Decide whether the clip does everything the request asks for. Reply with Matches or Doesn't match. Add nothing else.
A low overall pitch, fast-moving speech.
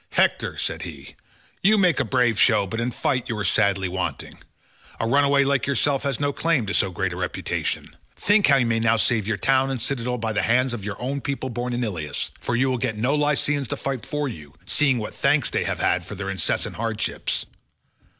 Matches